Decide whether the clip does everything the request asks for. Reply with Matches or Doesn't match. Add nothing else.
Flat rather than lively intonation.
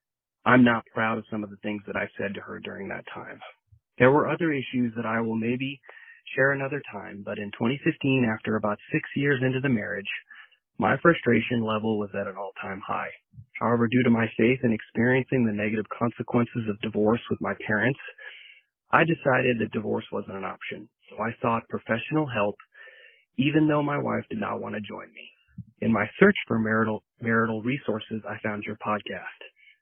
Doesn't match